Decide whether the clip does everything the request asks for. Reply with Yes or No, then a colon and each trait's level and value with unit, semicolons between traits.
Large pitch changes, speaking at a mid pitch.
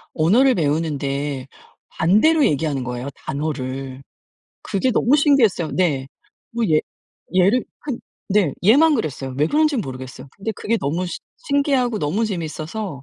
Yes: wide, 8.8 semitones; medium, 175 Hz